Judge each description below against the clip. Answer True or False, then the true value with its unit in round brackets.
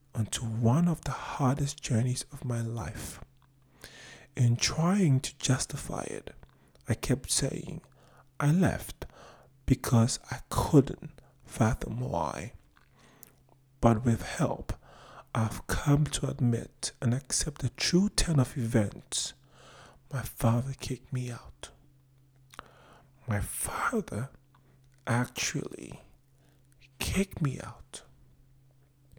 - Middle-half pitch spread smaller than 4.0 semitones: True (2.8 semitones)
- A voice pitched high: False (130 Hz)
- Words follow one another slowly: True (100 wpm)